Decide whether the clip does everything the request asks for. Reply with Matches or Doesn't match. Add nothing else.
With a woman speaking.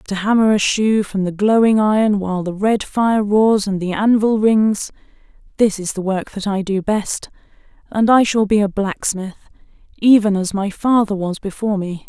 Matches